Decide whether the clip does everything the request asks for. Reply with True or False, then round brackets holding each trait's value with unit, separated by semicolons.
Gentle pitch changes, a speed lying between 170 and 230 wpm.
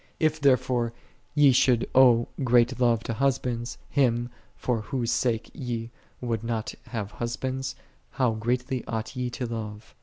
False (1.8 semitones; 145 wpm)